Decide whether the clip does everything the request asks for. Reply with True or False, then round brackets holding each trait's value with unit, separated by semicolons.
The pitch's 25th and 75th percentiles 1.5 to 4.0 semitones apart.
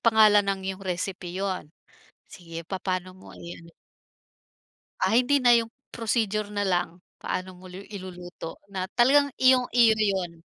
True (3.5 semitones)